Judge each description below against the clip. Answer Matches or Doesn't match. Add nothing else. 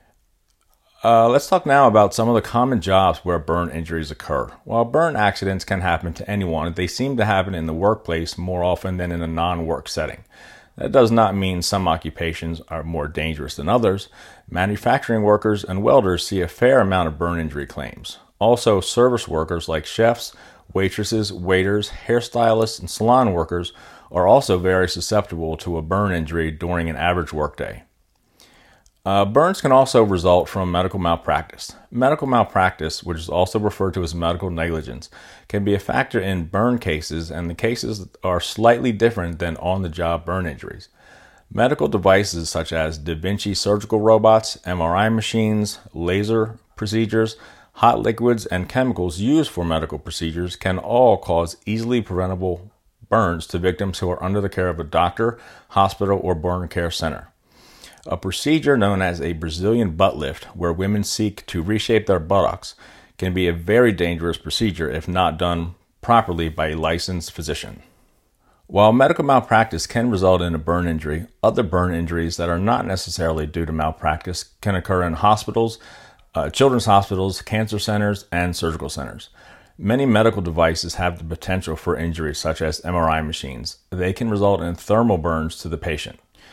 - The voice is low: Matches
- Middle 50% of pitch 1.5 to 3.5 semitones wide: Doesn't match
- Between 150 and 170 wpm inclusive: Matches